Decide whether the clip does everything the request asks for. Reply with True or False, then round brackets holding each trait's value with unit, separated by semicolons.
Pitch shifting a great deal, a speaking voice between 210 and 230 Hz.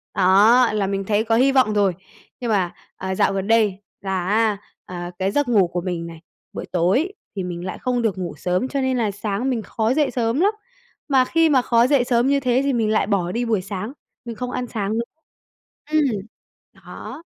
False (4.7 semitones; 220 Hz)